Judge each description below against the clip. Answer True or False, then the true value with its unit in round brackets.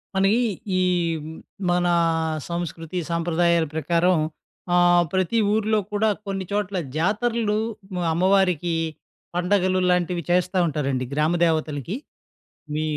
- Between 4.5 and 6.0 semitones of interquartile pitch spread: False (2.8 semitones)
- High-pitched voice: False (175 Hz)